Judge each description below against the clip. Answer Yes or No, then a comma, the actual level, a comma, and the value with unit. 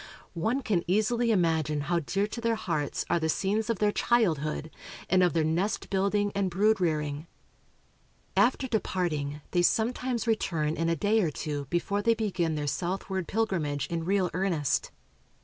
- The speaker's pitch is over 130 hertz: Yes, medium, 185 Hz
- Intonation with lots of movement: No, average, 5.0 semitones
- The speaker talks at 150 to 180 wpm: Yes, average, 165 wpm